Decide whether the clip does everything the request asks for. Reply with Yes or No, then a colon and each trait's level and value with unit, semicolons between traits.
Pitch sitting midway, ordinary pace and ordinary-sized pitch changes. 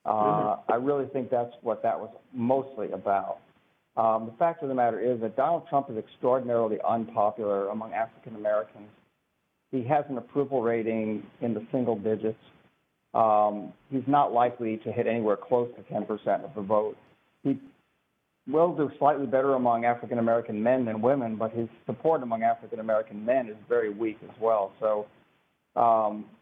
No: low, 115 Hz; average, 165 wpm; average, 3.4 semitones